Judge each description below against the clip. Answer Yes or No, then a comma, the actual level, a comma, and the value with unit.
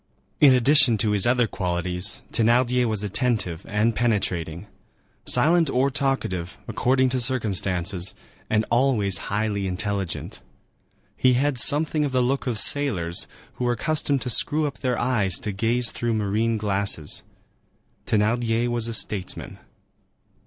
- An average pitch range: Yes, average, 4.1 semitones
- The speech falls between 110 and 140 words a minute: Yes, slow, 135 wpm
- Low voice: Yes, low, 115 Hz